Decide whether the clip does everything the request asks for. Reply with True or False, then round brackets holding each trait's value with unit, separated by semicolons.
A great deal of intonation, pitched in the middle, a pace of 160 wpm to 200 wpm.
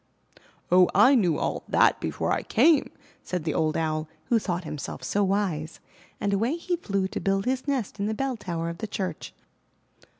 False (5.7 semitones; 195 Hz; 190 wpm)